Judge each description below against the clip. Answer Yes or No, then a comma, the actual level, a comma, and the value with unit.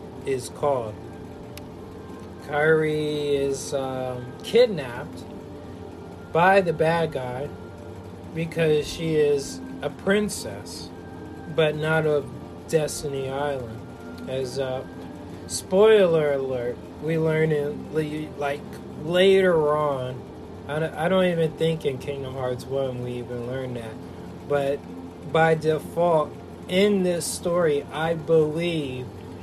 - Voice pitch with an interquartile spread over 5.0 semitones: Yes, wide, 5.4 semitones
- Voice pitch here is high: No, medium, 140 Hz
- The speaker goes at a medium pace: No, slow, 110 wpm